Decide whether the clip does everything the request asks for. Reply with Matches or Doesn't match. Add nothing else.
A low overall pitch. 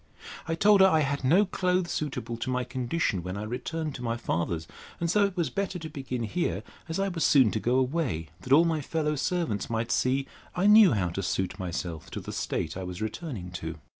Matches